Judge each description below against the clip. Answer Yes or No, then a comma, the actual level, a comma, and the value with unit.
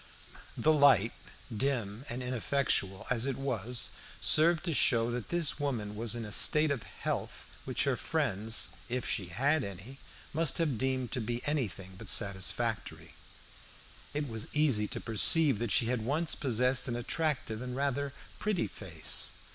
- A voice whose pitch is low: Yes, low, 125 Hz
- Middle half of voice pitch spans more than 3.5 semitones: Yes, average, 4.4 semitones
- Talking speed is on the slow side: No, average, 155 wpm